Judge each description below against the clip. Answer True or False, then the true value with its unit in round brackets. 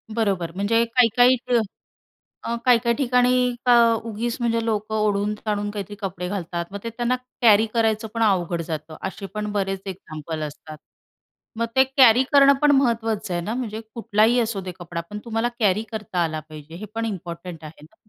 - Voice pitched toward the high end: True (215 Hz)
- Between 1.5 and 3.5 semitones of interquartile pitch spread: False (4.2 semitones)